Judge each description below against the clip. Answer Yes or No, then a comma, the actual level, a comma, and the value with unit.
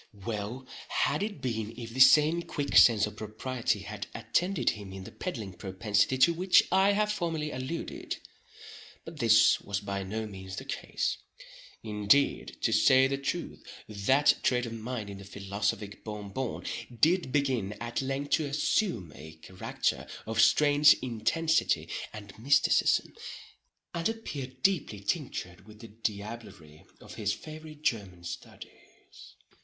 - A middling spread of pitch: No, wide, 6.0 semitones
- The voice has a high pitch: No, low, 115 Hz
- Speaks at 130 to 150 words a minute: Yes, average, 140 wpm